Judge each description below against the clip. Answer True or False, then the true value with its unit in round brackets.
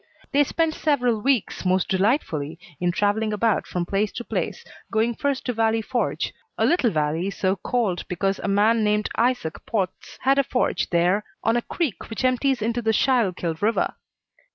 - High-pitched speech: True (220 Hz)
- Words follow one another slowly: False (175 wpm)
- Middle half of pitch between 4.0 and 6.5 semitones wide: True (4.5 semitones)